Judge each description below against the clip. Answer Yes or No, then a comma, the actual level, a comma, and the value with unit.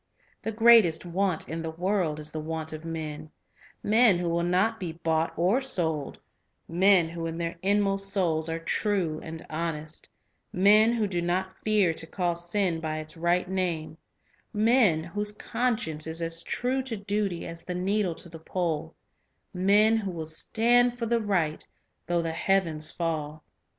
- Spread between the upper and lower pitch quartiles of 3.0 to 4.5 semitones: Yes, average, 4.0 semitones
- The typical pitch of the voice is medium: Yes, medium, 175 Hz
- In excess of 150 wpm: Yes, average, 170 wpm